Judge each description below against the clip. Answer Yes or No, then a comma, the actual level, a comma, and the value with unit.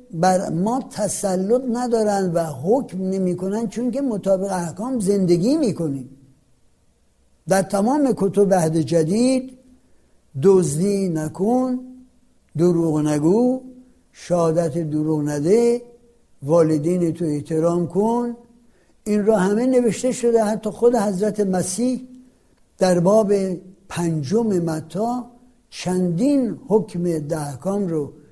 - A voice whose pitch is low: No, high, 195 Hz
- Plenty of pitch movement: Yes, wide, 6.0 semitones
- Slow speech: Yes, slow, 100 wpm